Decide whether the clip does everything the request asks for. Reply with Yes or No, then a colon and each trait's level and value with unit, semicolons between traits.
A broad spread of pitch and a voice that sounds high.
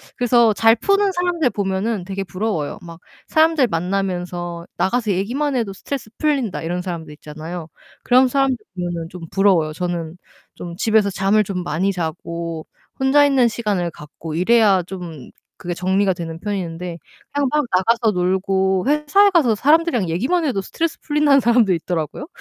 Yes: wide, 6.1 semitones; high, 195 Hz